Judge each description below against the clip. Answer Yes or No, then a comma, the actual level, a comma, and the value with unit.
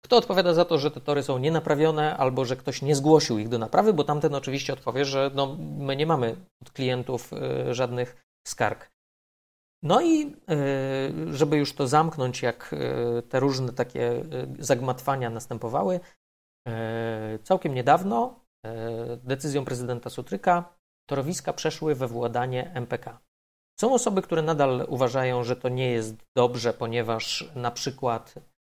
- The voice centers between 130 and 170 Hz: Yes, low, 135 Hz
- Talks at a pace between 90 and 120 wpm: No, average, 135 wpm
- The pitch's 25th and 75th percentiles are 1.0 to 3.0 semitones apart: No, average, 4.4 semitones